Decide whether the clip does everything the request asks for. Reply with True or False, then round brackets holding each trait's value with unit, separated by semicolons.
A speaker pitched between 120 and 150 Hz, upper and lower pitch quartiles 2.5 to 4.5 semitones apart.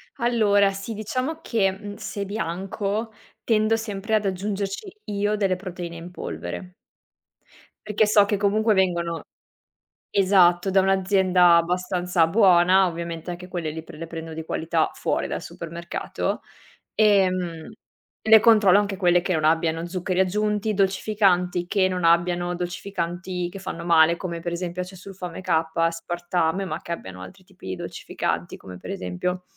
False (185 Hz; 2.8 semitones)